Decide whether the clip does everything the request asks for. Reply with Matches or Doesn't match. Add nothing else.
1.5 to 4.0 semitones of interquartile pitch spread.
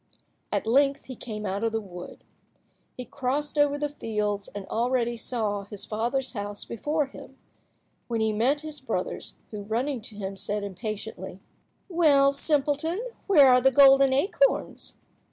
Doesn't match